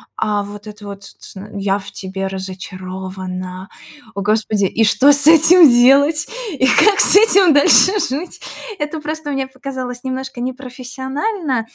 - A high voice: Yes, very high, 250 Hz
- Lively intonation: Yes, wide, 6.3 semitones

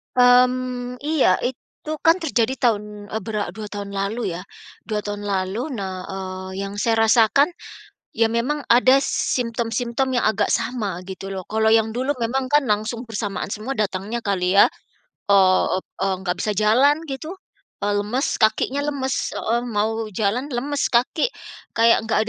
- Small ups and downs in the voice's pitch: No, average, 3.7 semitones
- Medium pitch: No, high, 225 Hz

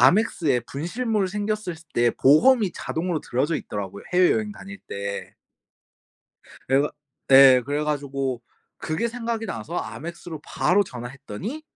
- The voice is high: No, medium, 160 Hz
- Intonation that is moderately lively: No, wide, 7.6 semitones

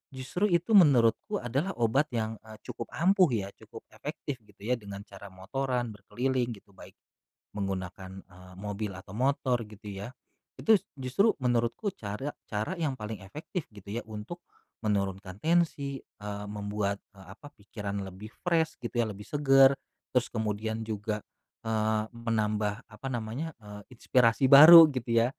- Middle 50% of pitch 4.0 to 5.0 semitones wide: Yes, average, 4.7 semitones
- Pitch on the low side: Yes, low, 110 Hz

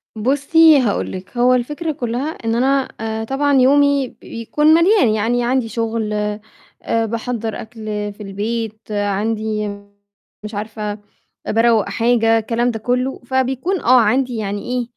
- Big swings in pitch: No, average, 3.2 semitones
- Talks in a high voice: Yes, high, 230 Hz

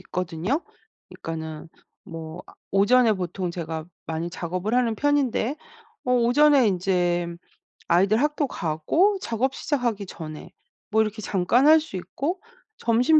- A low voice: No, high, 210 Hz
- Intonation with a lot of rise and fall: Yes, wide, 6.5 semitones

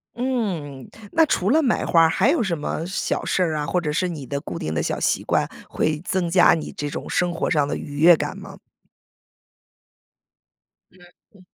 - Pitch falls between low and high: Yes, medium, 170 Hz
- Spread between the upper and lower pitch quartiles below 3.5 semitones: No, average, 4.1 semitones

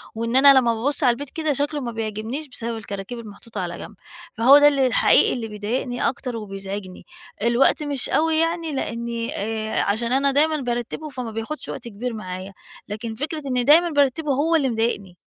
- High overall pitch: Yes, high, 240 Hz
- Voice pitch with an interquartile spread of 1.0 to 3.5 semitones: No, average, 4.5 semitones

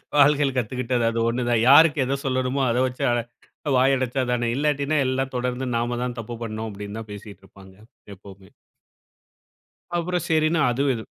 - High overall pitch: No, low, 125 Hz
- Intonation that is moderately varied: Yes, average, 3.2 semitones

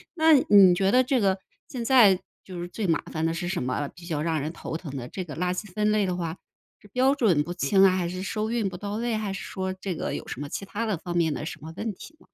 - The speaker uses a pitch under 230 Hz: Yes, high, 190 Hz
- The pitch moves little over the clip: No, average, 4.0 semitones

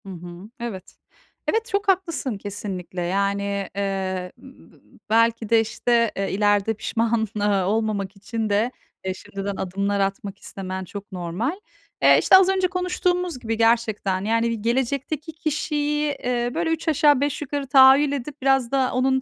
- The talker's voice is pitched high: Yes, high, 230 Hz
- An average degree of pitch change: No, wide, 5.9 semitones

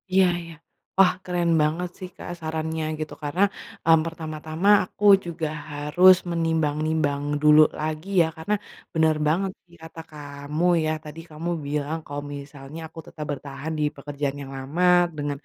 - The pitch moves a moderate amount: No, narrow, 2.1 semitones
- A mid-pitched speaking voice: Yes, medium, 155 Hz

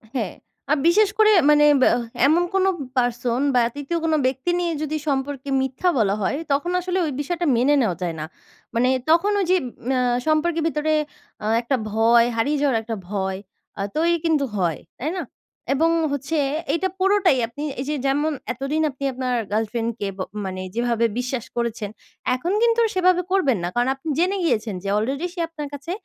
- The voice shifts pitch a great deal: Yes, wide, 5.8 semitones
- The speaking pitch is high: Yes, very high, 275 Hz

